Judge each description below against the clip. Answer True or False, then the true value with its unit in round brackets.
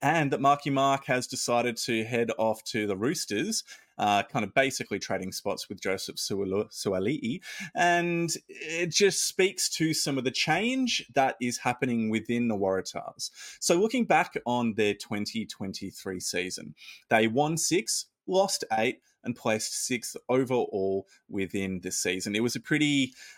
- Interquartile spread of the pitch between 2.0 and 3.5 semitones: False (5.0 semitones)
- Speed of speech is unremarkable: True (150 wpm)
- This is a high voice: False (120 Hz)